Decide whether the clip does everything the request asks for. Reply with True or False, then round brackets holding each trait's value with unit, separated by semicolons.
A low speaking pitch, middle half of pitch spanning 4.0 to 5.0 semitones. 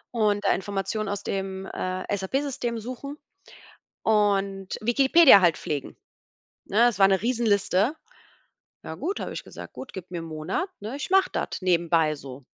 False (200 Hz; 4.4 semitones)